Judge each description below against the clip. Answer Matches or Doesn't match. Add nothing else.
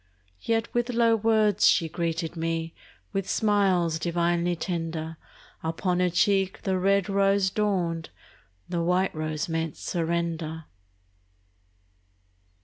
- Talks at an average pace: Doesn't match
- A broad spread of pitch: Doesn't match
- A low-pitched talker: Doesn't match